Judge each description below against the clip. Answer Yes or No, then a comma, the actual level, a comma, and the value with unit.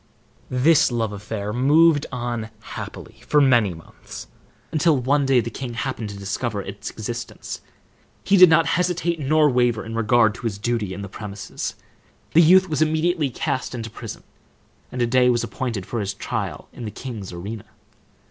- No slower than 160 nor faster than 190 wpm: Yes, average, 170 wpm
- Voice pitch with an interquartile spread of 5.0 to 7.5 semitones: Yes, average, 5.3 semitones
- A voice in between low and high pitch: No, low, 120 Hz